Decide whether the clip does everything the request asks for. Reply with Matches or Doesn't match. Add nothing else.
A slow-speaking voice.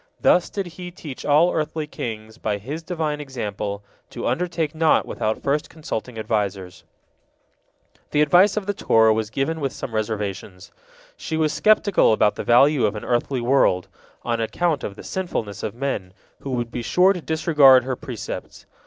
Doesn't match